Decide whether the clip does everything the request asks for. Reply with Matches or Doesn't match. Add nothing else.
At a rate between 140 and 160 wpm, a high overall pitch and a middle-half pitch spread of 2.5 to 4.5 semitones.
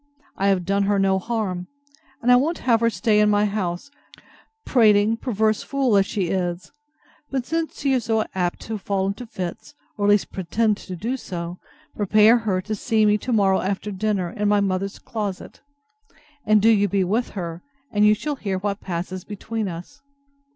Doesn't match